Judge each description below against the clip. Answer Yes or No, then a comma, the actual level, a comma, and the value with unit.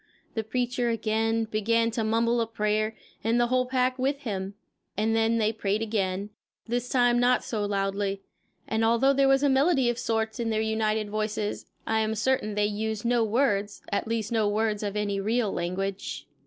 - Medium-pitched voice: No, high, 220 Hz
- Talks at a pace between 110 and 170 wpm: No, average, 185 wpm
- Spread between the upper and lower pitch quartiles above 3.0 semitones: No, narrow, 2.4 semitones